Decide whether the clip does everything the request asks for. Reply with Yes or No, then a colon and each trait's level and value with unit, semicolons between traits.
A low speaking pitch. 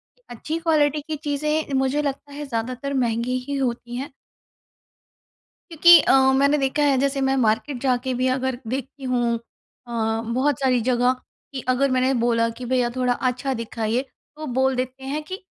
No: very high, 260 Hz